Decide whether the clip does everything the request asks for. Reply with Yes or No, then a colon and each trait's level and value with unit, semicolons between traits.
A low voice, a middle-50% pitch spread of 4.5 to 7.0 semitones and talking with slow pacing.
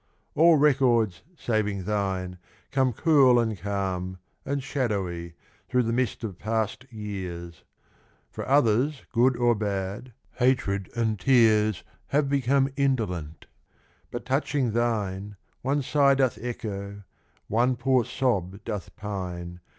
Yes: low, 110 Hz; average, 4.9 semitones; slow, 120 wpm